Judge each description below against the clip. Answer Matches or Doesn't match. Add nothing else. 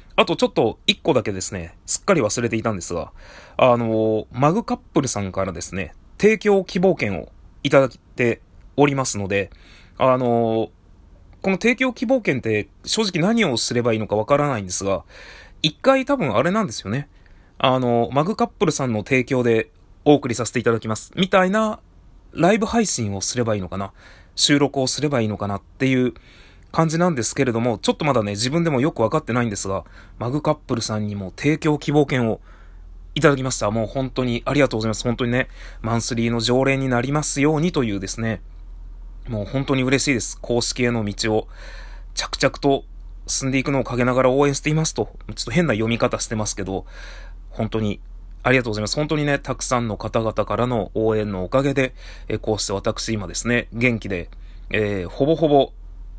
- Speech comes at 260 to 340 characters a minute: Doesn't match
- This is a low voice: Matches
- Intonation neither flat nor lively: Doesn't match